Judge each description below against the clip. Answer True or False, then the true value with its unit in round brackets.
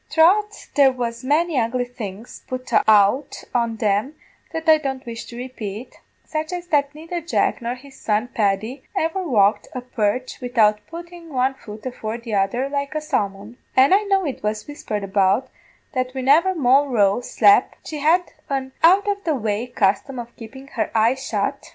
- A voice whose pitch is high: True (255 Hz)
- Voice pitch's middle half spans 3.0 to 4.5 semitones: False (5.5 semitones)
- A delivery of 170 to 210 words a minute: True (175 wpm)